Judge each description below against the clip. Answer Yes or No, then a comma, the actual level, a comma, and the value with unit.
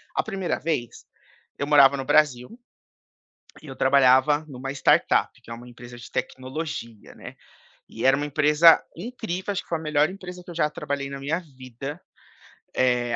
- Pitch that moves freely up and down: No, average, 3.9 semitones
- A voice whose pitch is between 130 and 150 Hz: Yes, medium, 140 Hz